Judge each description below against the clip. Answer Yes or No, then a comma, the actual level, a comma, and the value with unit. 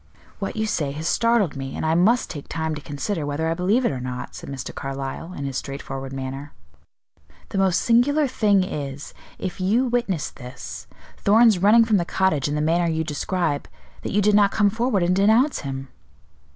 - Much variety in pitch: Yes, wide, 6.6 semitones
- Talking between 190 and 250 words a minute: Yes, average, 195 wpm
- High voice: No, medium, 175 Hz